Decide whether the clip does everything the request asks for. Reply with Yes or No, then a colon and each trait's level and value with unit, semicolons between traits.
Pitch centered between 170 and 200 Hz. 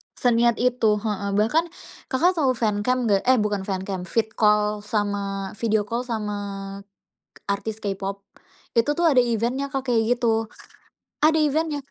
No: high, 225 Hz